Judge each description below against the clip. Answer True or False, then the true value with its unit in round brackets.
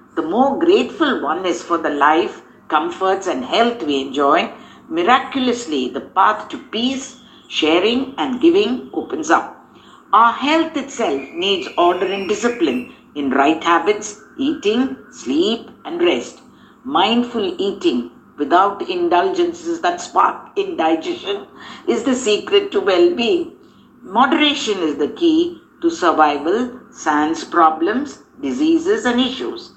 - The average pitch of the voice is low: False (265 Hz)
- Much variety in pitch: True (8.7 semitones)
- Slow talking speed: True (125 wpm)